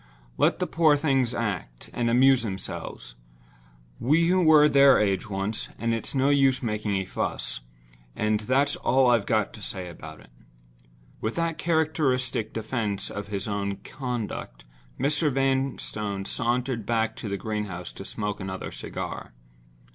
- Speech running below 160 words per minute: Yes, average, 140 wpm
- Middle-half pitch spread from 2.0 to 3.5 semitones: No, average, 5.1 semitones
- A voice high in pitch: No, low, 115 Hz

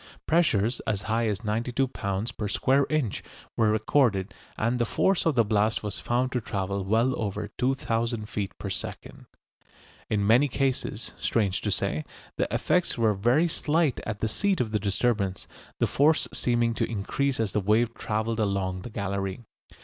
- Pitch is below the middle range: Yes, low, 110 Hz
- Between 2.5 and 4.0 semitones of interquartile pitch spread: Yes, average, 3.5 semitones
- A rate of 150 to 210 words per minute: Yes, average, 170 wpm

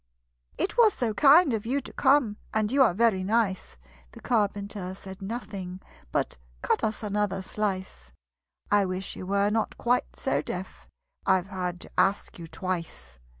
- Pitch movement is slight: No, average, 3.4 semitones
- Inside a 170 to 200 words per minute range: No, average, 160 wpm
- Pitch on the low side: No, high, 200 Hz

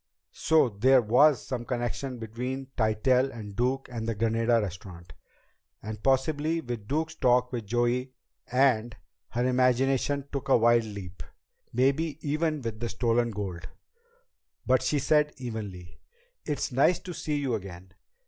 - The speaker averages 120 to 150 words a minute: Yes, average, 140 wpm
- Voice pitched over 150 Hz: No, low, 120 Hz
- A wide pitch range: No, average, 3.5 semitones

